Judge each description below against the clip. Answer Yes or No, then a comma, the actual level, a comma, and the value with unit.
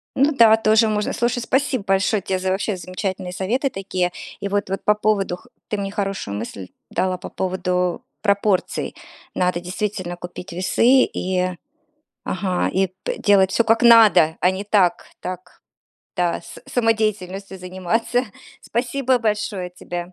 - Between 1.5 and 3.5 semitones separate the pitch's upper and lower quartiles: Yes, average, 3.1 semitones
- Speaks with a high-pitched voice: Yes, high, 195 Hz